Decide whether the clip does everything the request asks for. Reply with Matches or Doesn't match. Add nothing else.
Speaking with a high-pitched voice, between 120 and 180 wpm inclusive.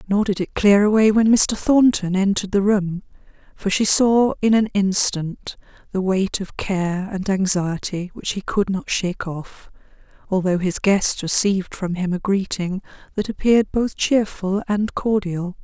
Matches